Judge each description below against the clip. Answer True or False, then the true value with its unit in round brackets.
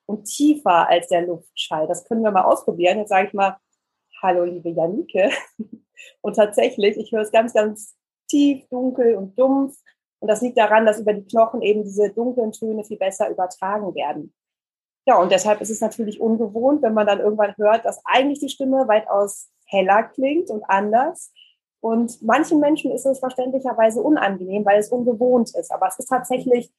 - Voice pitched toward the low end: False (220 Hz)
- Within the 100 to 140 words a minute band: False (180 wpm)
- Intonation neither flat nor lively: True (3.8 semitones)